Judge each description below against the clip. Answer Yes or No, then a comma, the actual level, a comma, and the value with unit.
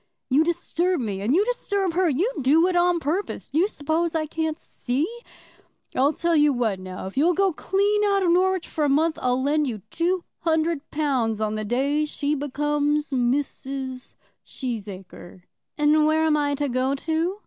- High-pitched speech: Yes, very high, 300 Hz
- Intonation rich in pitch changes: No, average, 4.5 semitones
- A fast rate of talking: No, average, 180 wpm